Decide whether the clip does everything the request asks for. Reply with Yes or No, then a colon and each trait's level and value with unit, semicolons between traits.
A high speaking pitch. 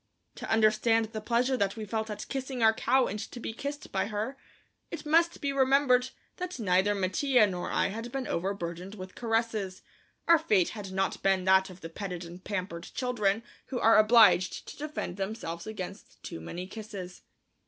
Yes: high, 215 Hz